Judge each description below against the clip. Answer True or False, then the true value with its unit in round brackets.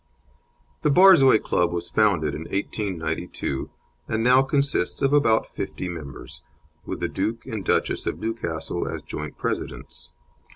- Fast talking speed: False (135 wpm)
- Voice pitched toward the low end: True (110 Hz)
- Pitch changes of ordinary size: False (7.7 semitones)